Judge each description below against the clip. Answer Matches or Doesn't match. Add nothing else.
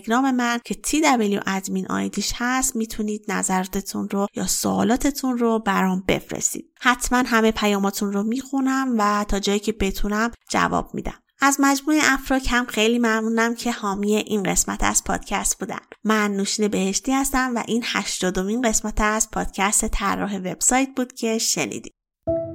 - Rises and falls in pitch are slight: Doesn't match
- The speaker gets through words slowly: Doesn't match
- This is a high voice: Matches